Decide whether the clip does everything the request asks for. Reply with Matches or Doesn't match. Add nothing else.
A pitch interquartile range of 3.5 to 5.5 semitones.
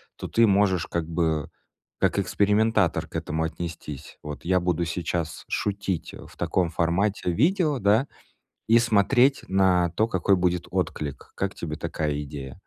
Matches